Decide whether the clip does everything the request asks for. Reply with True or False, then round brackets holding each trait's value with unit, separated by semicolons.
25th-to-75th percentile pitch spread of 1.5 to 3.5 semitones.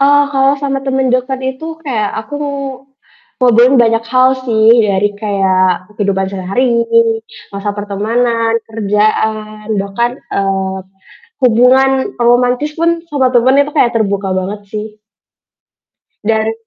False (4.0 semitones)